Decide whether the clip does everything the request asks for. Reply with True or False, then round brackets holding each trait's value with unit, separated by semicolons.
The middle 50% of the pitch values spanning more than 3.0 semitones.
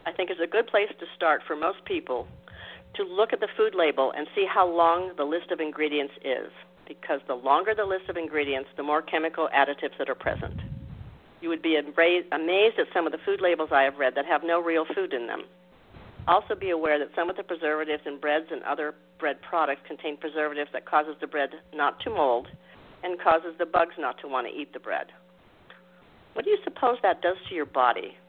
True (3.8 semitones)